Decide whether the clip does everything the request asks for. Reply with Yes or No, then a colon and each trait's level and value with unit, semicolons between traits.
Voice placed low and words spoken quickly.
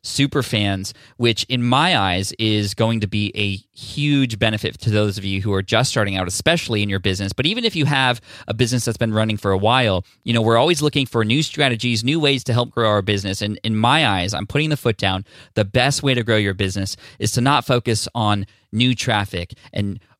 Yes: low, 115 Hz; fast, 230 wpm